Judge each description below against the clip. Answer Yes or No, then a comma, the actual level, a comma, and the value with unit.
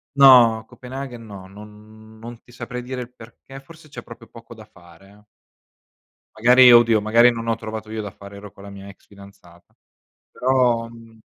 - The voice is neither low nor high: No, low, 115 Hz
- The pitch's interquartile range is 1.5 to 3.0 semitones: Yes, average, 2.7 semitones